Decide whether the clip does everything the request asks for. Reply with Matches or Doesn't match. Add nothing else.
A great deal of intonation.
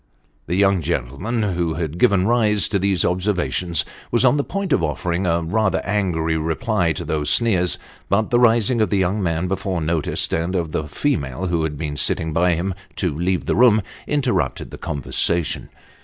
Doesn't match